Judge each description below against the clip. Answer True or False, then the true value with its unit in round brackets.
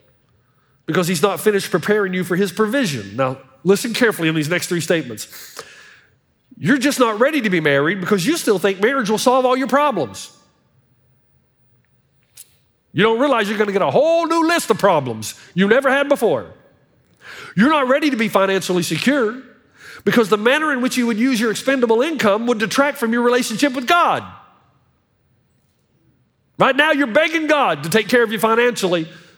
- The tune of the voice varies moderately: False (7.3 semitones)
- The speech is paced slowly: False (175 wpm)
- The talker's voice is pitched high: True (220 Hz)